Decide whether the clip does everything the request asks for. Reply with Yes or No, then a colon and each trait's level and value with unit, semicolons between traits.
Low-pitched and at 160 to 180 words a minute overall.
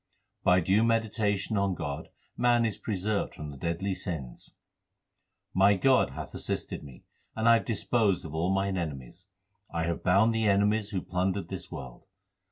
Yes: very low, 95 Hz; average, 165 wpm